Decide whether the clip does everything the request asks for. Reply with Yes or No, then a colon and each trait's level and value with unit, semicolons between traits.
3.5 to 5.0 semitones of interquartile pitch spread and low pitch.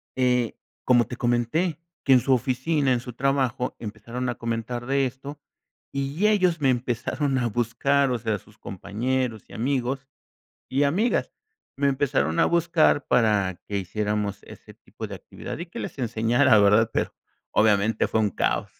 Yes: average, 3.8 semitones; low, 125 Hz